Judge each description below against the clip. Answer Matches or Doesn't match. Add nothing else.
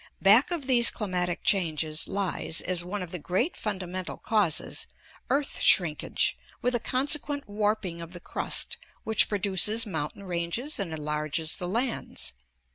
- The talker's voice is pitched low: Doesn't match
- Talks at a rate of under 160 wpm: Matches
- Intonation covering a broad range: Doesn't match